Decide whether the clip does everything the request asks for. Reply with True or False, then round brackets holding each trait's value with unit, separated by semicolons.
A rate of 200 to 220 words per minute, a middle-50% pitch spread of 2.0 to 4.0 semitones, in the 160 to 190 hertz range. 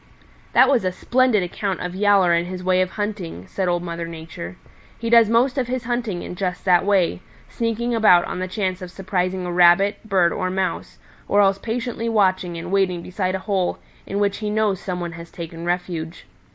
True (205 wpm; 2.9 semitones; 185 Hz)